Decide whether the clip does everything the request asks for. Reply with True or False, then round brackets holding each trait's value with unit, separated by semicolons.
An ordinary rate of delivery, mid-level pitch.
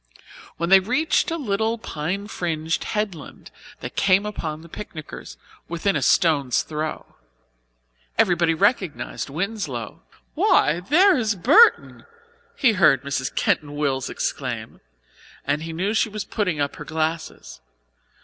False (130 wpm; 175 Hz)